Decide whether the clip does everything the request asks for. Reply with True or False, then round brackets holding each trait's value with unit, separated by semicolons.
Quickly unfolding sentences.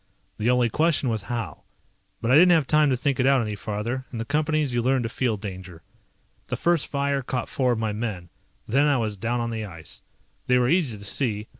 True (230 wpm)